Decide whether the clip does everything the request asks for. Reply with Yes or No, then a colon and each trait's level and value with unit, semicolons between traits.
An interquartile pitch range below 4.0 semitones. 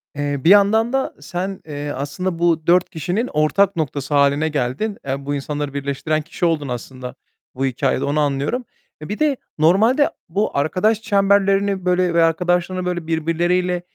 No: average, 5.1 semitones